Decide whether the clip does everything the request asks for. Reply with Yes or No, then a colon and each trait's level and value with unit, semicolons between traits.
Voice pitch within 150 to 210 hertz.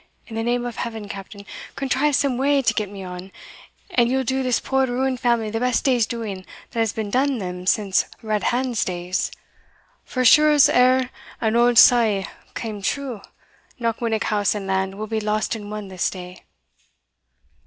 No: high, 225 Hz